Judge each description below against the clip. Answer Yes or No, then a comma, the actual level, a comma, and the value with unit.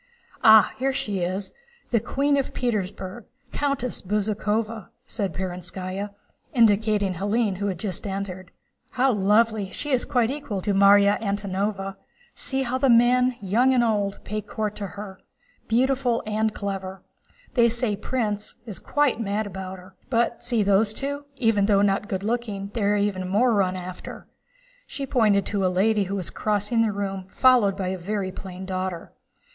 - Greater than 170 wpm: No, average, 160 wpm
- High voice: Yes, high, 205 Hz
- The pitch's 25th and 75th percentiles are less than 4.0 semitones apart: Yes, average, 3.3 semitones